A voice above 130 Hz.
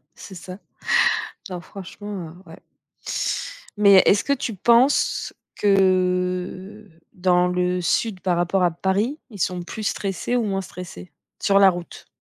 Yes: high, 190 Hz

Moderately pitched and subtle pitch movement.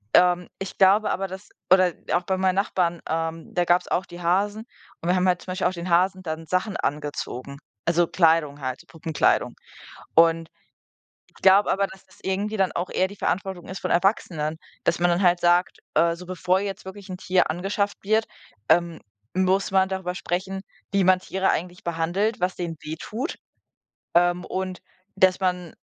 Yes: medium, 180 Hz; narrow, 2.0 semitones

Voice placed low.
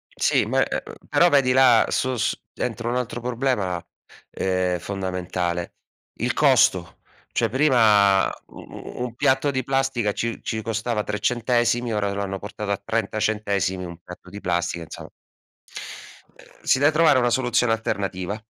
Yes: low, 110 Hz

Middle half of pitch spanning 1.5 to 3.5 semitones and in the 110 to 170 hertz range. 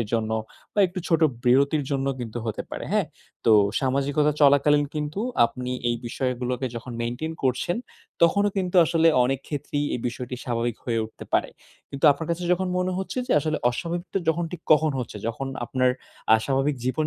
No: average, 4.5 semitones; medium, 140 Hz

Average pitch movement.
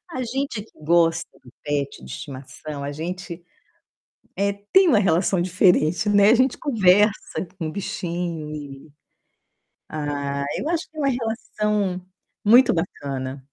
No: wide, 6.1 semitones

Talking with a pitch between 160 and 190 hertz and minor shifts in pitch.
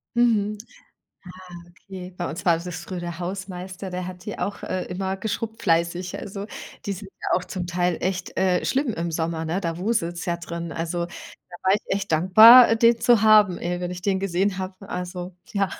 Yes: medium, 185 Hz; narrow, 2.3 semitones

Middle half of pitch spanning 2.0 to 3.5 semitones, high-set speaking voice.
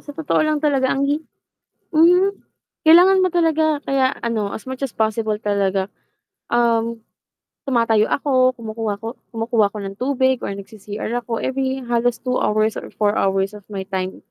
No: average, 4.6 semitones; high, 235 Hz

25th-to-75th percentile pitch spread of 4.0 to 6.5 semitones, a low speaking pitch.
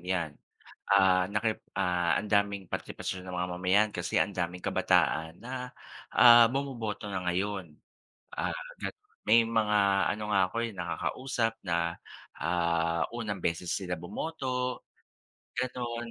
Yes: average, 4.6 semitones; low, 100 Hz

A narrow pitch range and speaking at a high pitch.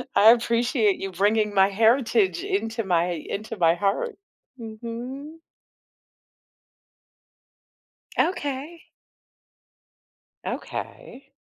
No: wide, 5.4 semitones; high, 230 Hz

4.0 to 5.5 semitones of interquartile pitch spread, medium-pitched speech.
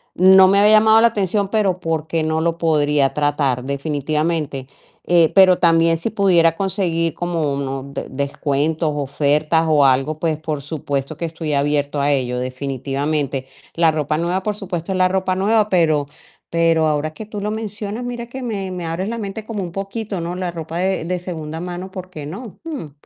Yes: average, 4.4 semitones; medium, 165 Hz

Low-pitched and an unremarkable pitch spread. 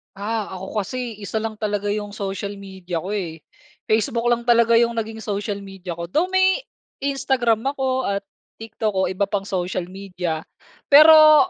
No: high, 210 Hz; average, 3.5 semitones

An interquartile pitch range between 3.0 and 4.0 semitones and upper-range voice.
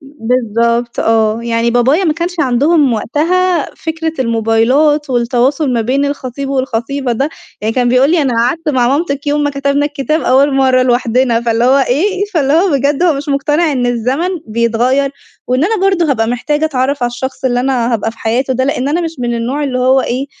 Yes: average, 3.5 semitones; very high, 265 Hz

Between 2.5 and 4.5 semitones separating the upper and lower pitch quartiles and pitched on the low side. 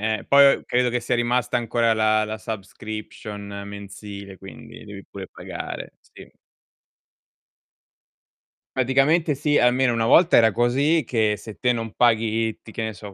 Yes: average, 2.8 semitones; low, 115 Hz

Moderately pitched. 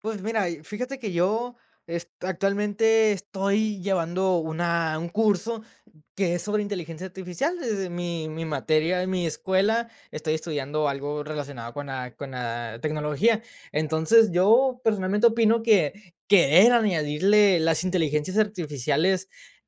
Yes: medium, 180 Hz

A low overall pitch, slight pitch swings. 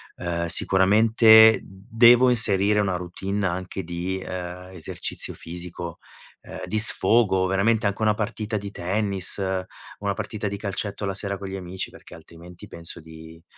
No: very low, 95 Hz; average, 3.1 semitones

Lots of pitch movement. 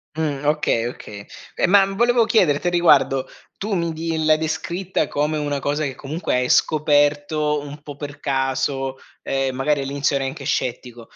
No: average, 2.7 semitones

